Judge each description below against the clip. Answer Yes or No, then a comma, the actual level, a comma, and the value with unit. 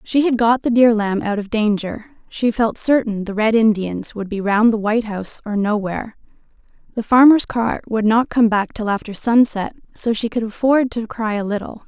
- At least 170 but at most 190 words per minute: No, fast, 205 wpm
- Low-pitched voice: No, high, 220 Hz